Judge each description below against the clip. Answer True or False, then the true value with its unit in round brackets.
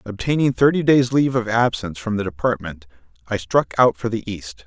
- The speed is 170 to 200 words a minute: True (195 wpm)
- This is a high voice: False (110 Hz)